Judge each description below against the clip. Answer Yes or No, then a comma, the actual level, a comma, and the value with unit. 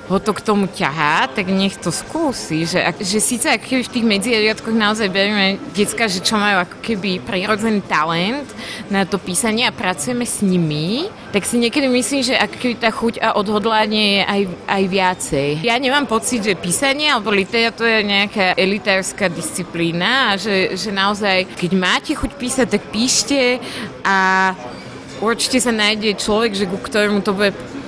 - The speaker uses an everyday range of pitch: Yes, average, 3.3 semitones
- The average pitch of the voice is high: Yes, high, 210 Hz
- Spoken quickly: Yes, fast, 170 wpm